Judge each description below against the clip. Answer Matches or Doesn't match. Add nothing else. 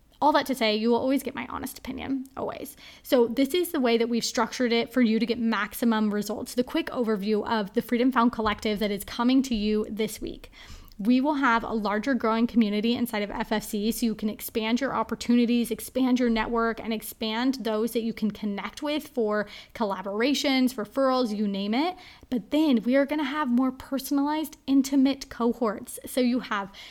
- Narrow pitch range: Doesn't match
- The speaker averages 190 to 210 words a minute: Matches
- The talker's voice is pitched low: Doesn't match